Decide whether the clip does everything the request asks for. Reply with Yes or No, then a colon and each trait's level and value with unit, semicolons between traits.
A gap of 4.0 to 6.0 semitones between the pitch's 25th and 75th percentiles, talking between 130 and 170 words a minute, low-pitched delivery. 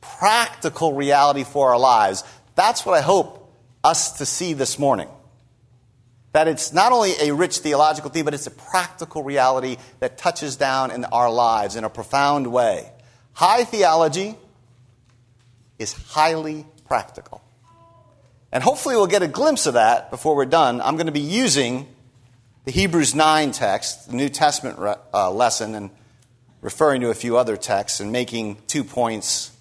Yes: average, 4.3 semitones; average, 160 wpm; low, 130 Hz